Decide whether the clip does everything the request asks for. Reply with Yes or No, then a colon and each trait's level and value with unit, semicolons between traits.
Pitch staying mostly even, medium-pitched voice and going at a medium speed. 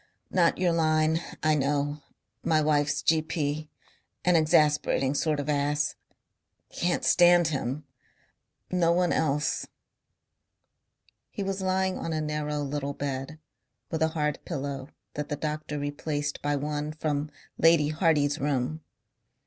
No: narrow, 1.8 semitones; medium, 150 Hz; slow, 125 wpm